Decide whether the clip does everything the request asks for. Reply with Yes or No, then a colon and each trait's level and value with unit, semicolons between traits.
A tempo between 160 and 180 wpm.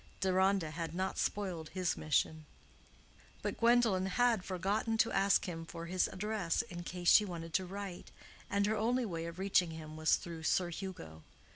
Yes: average, 170 wpm